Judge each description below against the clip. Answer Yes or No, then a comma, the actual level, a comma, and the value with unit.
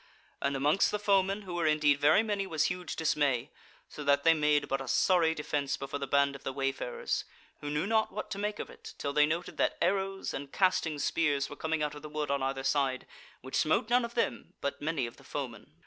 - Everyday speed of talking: No, fast, 230 wpm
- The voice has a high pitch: No, medium, 150 Hz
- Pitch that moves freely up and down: No, average, 4.7 semitones